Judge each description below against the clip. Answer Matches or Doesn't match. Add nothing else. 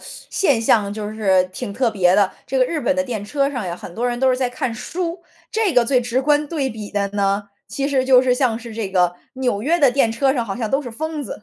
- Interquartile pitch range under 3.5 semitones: Doesn't match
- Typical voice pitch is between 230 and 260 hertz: Matches